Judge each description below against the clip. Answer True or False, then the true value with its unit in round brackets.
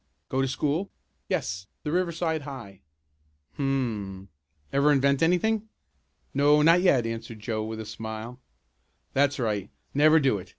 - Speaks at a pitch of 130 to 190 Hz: True (135 Hz)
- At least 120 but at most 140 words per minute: True (135 wpm)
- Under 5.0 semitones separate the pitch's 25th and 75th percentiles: False (5.3 semitones)